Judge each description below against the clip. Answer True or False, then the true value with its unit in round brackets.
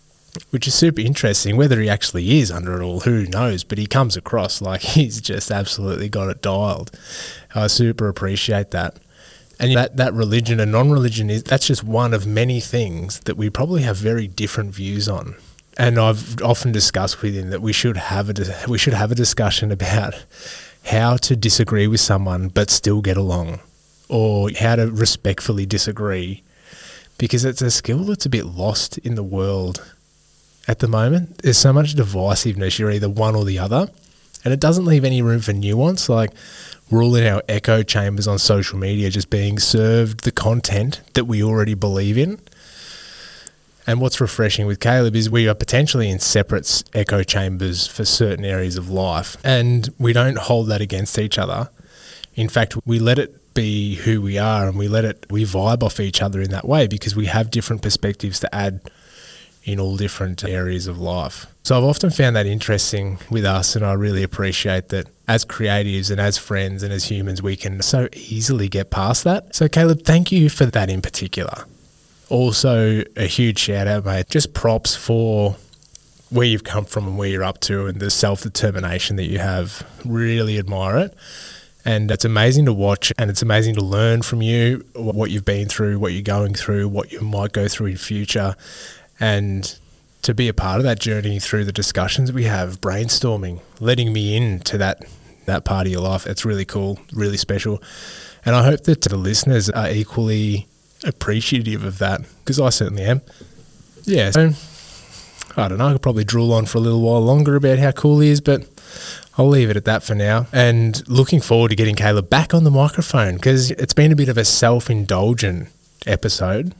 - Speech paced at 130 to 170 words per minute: False (190 wpm)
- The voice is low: True (110 Hz)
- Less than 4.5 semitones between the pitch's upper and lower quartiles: True (3.4 semitones)